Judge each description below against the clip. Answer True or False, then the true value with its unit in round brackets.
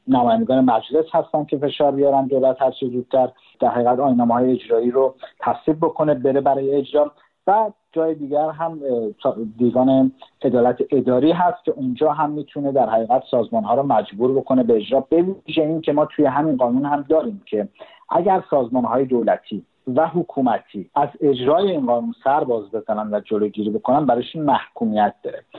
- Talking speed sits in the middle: False (165 wpm)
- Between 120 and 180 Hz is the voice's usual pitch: True (135 Hz)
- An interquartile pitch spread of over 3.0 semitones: True (3.8 semitones)